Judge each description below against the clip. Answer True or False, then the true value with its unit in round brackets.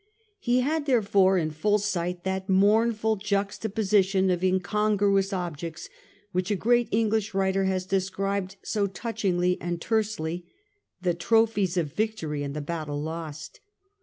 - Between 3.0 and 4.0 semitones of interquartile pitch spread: True (3.3 semitones)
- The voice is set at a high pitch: True (195 Hz)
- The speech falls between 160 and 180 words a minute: False (135 wpm)